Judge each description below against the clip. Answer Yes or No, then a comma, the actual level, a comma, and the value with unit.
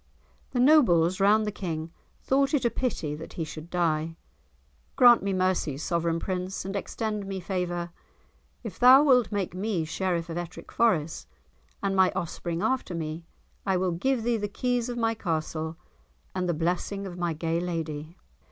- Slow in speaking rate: No, average, 170 wpm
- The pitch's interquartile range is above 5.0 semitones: No, average, 4.5 semitones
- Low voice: No, medium, 185 Hz